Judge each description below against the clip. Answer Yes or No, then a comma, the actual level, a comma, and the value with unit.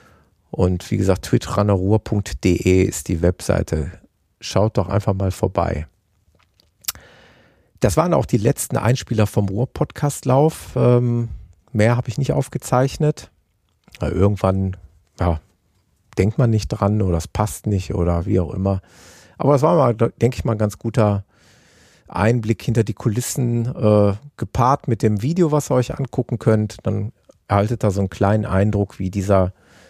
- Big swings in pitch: No, average, 4.2 semitones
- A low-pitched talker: Yes, low, 105 Hz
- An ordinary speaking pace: Yes, average, 150 wpm